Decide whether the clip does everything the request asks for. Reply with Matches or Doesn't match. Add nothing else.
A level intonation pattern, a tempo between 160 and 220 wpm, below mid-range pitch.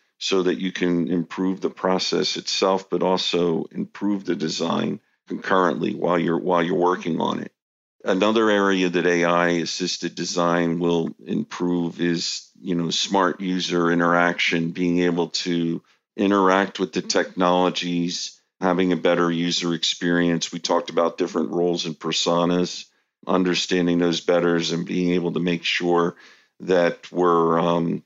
Doesn't match